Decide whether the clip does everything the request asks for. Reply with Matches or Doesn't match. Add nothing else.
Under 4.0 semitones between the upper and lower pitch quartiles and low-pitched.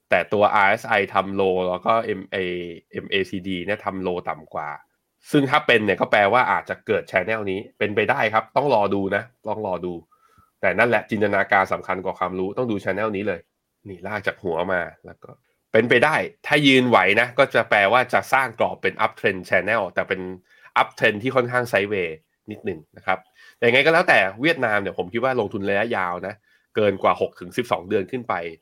Doesn't match